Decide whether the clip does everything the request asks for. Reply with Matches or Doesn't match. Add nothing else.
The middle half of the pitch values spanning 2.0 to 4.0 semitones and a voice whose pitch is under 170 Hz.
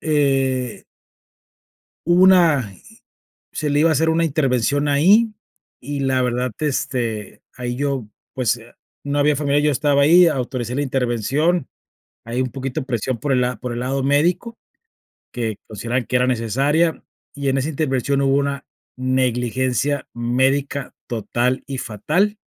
Matches